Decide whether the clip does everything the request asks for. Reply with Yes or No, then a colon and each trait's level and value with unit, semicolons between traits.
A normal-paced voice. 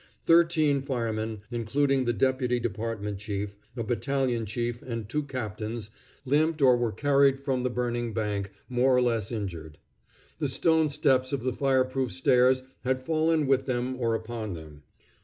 Yes: average, 160 wpm